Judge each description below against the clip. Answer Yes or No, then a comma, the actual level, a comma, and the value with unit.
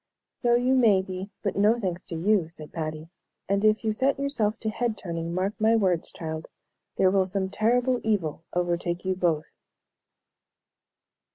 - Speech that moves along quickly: No, average, 165 wpm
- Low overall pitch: No, high, 195 Hz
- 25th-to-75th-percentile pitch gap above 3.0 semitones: Yes, average, 4.2 semitones